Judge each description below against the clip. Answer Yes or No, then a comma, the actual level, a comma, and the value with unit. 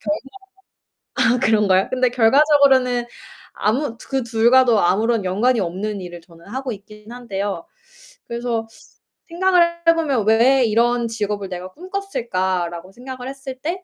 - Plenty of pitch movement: No, average, 4.6 semitones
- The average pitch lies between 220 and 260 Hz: Yes, high, 235 Hz